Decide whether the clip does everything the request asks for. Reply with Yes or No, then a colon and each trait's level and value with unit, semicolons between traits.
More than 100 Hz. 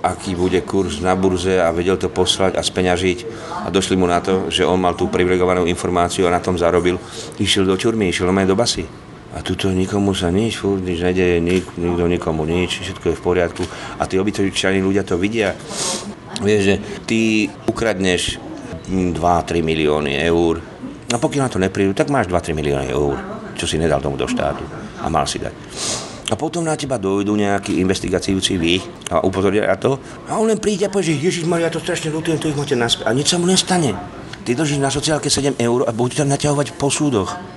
No: very low, 95 Hz